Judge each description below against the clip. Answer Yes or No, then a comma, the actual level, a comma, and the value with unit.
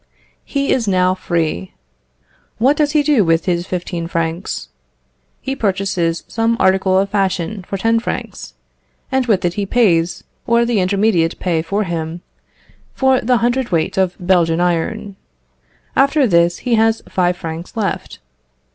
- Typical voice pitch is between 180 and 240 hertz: Yes, high, 190 Hz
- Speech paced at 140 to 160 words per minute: Yes, average, 145 wpm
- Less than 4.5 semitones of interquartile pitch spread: No, average, 4.9 semitones